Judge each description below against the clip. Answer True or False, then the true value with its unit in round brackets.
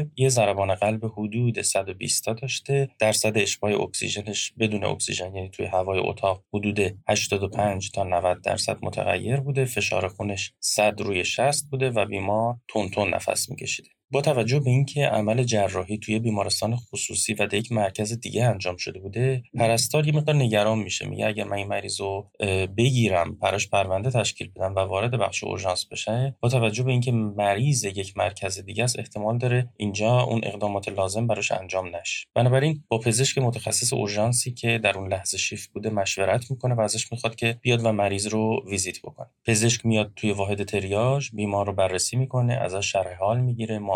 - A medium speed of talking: False (175 wpm)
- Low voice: True (110 Hz)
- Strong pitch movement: False (3.2 semitones)